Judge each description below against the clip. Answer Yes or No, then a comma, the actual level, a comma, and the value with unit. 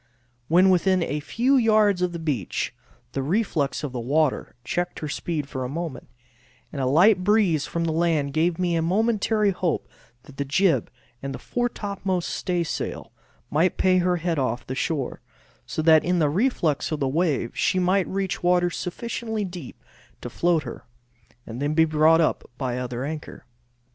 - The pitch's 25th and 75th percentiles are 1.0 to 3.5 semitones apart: No, average, 4.1 semitones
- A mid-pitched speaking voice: Yes, medium, 170 Hz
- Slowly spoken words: No, average, 175 wpm